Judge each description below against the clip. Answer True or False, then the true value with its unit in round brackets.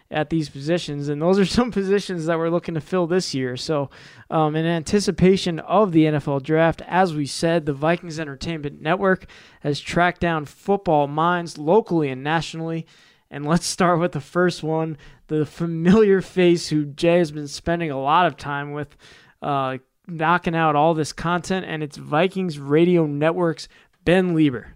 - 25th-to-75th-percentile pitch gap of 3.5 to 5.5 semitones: False (2.9 semitones)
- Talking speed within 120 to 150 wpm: False (170 wpm)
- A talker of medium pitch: True (165 Hz)